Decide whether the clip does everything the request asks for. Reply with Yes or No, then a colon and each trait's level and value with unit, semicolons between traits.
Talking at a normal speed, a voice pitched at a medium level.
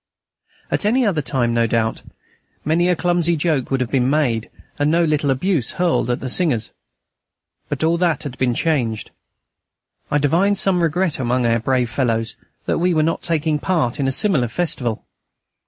Yes: average, 175 wpm; medium, 145 Hz